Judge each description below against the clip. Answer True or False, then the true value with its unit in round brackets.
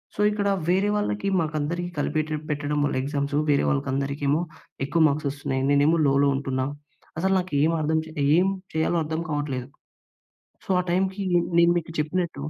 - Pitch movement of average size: True (3.4 semitones)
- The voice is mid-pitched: True (150 Hz)